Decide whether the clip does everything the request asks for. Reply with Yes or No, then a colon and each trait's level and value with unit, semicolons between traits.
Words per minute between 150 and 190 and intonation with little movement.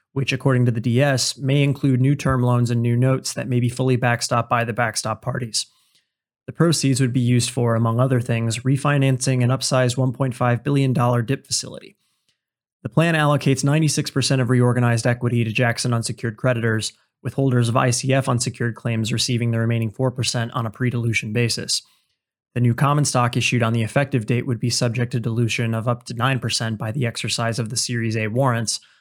Yes: average, 185 wpm; narrow, 2.0 semitones